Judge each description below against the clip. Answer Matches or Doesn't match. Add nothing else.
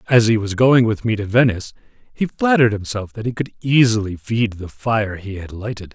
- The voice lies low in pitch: Matches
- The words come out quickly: Matches